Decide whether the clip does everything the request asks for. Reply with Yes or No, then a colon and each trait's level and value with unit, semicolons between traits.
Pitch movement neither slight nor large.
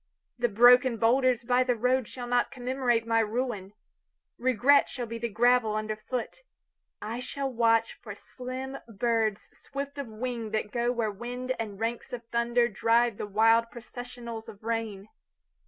No: narrow, 2.0 semitones